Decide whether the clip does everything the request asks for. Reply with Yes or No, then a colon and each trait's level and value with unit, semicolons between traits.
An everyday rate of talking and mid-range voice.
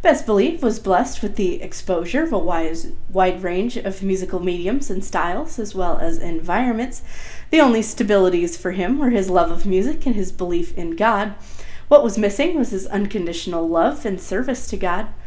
No: average, 180 wpm; high, 195 Hz